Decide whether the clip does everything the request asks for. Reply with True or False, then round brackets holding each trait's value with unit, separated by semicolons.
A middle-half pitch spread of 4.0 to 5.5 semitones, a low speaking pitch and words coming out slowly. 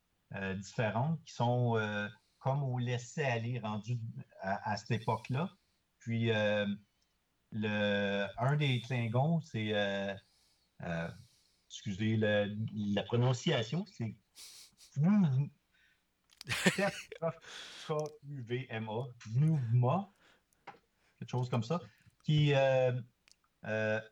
True (4.5 semitones; 120 Hz; 95 wpm)